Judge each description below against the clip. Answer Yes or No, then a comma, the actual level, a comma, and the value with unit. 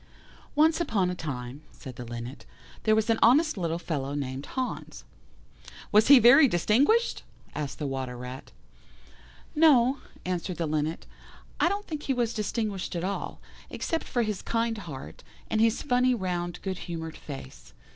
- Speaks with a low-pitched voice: No, high, 190 Hz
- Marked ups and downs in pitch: Yes, wide, 8.4 semitones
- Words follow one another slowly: No, average, 155 wpm